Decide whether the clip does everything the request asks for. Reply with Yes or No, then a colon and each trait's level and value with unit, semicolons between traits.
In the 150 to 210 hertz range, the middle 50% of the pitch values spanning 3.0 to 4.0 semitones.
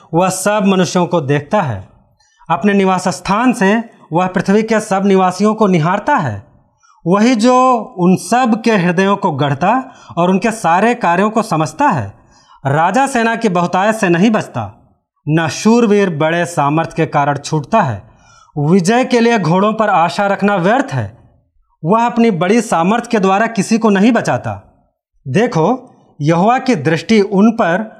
No: high, 190 Hz; wide, 5.5 semitones